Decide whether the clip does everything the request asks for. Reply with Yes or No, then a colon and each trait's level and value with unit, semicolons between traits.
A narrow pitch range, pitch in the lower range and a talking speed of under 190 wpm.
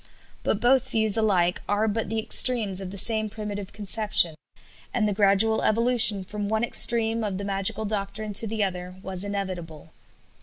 No: narrow, 2.1 semitones; high, 210 Hz; average, 165 wpm